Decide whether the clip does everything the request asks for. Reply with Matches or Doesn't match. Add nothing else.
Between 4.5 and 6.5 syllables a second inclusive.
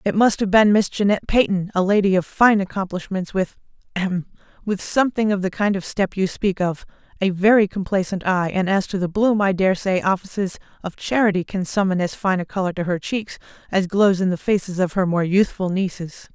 Matches